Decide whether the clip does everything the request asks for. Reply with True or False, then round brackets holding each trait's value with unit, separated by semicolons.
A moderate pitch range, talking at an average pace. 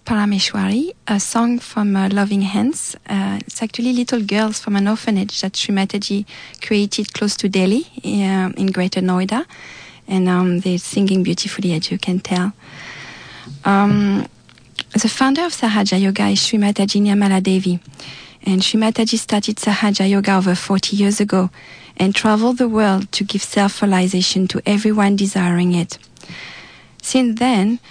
False (2.1 semitones; 145 wpm)